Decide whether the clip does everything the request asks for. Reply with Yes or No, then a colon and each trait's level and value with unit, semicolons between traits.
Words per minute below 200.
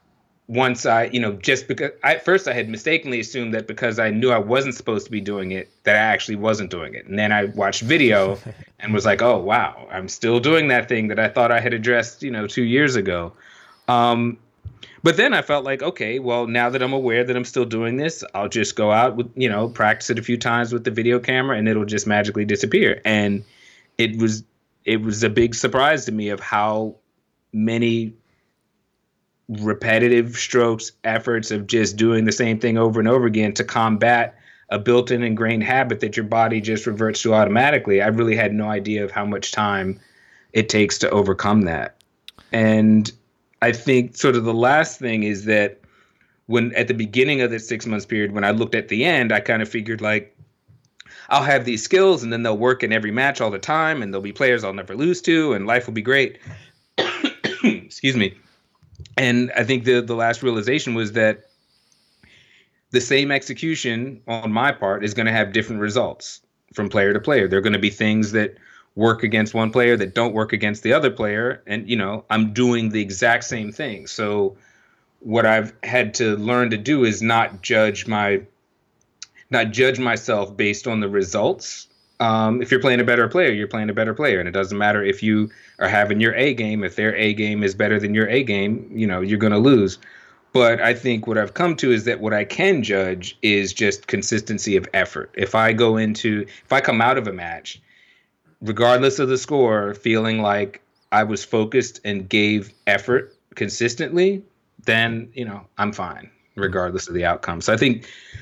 No: fast, 205 wpm